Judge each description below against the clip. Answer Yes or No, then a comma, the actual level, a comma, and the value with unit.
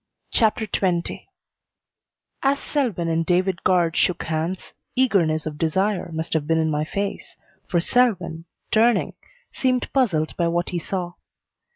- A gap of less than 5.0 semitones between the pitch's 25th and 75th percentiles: Yes, average, 4.2 semitones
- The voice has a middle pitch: Yes, medium, 175 Hz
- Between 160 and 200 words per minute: No, average, 140 wpm